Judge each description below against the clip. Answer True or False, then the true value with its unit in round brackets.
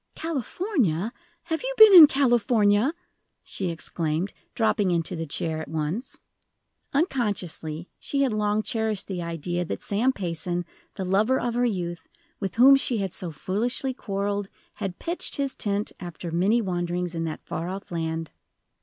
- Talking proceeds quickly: False (155 wpm)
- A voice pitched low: False (200 Hz)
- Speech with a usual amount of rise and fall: False (5.8 semitones)